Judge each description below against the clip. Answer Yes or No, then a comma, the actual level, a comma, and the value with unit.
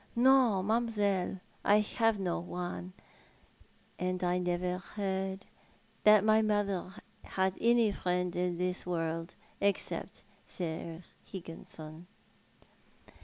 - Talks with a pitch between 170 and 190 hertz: Yes, medium, 185 Hz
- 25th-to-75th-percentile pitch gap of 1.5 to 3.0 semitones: Yes, average, 2.7 semitones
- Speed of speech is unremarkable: No, slow, 105 wpm